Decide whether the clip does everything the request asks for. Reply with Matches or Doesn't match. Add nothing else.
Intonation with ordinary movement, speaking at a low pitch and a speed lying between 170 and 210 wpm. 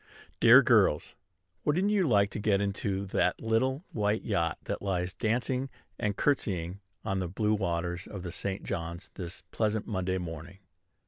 Doesn't match